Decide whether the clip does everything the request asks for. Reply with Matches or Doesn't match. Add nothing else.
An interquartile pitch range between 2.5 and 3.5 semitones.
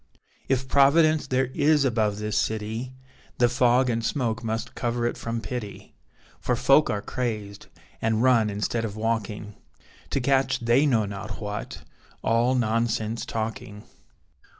Matches